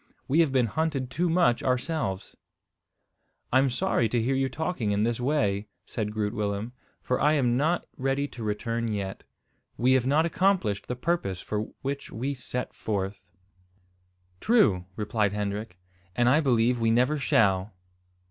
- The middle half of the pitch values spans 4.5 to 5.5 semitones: Yes, average, 4.9 semitones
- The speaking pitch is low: Yes, low, 120 Hz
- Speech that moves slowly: No, average, 155 wpm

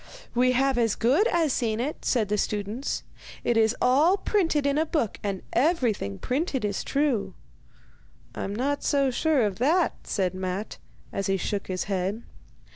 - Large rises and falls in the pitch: Yes, wide, 5.9 semitones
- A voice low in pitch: No, high, 240 Hz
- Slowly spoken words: No, average, 165 wpm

